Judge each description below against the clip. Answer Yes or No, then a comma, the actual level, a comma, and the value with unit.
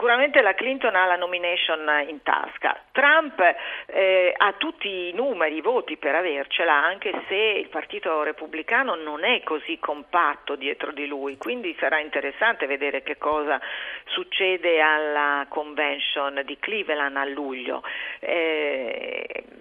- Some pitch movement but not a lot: No, wide, 8.0 semitones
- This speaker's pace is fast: No, average, 135 wpm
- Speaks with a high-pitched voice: No, medium, 160 Hz